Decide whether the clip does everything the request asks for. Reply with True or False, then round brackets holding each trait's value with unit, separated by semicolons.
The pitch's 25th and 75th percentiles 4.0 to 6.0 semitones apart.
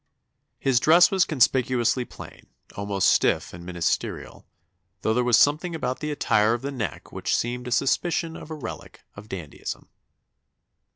True (5.5 semitones)